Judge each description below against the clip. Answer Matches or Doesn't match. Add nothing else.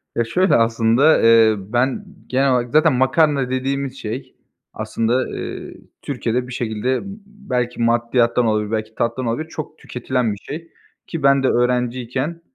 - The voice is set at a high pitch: Doesn't match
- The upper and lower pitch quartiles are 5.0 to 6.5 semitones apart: Doesn't match